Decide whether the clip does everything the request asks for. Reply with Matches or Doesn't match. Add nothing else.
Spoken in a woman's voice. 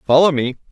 Doesn't match